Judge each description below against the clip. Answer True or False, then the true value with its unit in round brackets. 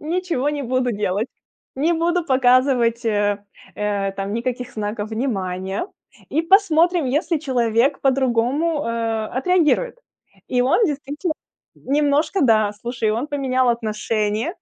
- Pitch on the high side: True (255 Hz)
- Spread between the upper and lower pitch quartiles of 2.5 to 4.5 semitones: False (5.3 semitones)